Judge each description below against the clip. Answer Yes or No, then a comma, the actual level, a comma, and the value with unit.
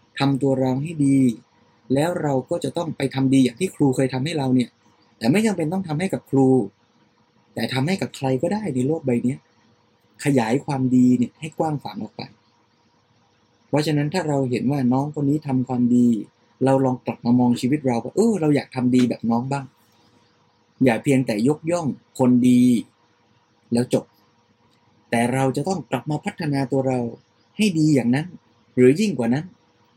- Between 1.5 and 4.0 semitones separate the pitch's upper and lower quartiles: Yes, average, 3.3 semitones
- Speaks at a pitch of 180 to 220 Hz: No, low, 130 Hz